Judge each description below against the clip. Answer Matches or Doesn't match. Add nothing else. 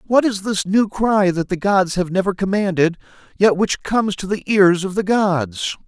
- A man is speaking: Matches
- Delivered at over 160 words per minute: Matches